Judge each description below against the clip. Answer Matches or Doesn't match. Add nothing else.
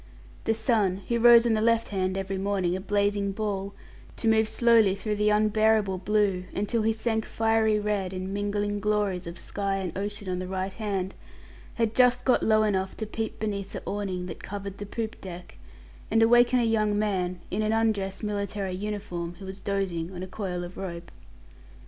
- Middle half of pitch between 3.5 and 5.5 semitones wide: Doesn't match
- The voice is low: Doesn't match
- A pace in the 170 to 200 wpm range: Matches